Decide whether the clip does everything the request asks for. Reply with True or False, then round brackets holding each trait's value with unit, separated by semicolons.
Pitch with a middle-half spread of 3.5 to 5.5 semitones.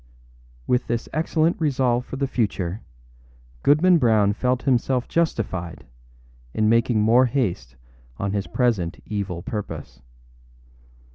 True (4.5 semitones)